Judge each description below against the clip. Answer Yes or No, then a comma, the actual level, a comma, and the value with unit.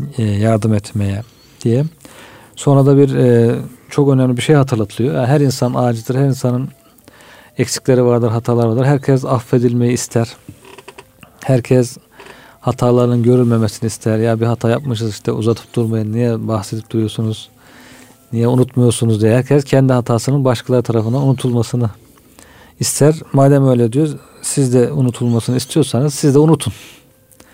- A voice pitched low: Yes, low, 125 Hz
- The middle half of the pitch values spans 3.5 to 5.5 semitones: No, narrow, 2.5 semitones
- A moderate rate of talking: Yes, average, 125 wpm